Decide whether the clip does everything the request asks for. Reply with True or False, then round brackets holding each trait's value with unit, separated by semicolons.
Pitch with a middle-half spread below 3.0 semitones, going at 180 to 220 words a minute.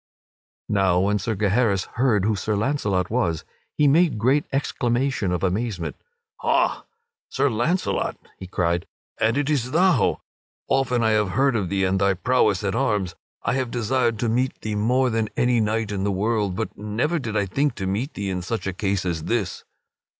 False (4.5 semitones; 185 wpm)